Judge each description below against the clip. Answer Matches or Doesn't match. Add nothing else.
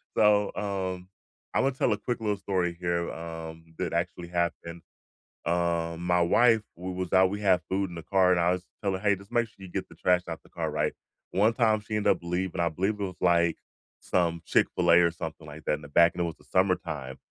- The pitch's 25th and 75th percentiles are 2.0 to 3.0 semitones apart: Matches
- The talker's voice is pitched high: Doesn't match